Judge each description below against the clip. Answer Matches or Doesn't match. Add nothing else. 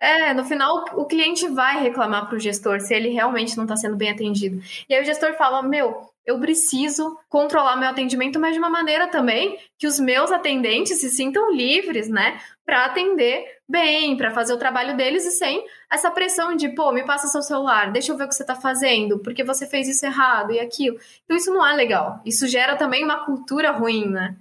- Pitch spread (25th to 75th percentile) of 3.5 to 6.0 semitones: Matches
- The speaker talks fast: Matches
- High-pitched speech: Matches